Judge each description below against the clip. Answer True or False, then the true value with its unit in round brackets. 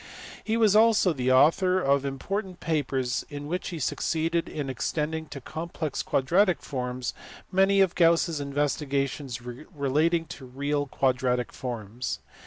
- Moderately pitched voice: True (145 Hz)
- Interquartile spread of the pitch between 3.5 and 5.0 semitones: True (4.4 semitones)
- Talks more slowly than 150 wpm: True (135 wpm)